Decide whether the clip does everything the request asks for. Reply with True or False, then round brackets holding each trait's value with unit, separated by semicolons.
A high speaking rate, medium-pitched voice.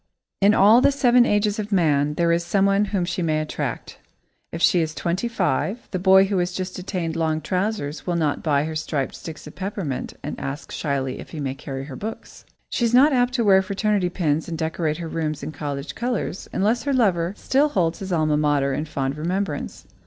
True (210 wpm; 175 Hz)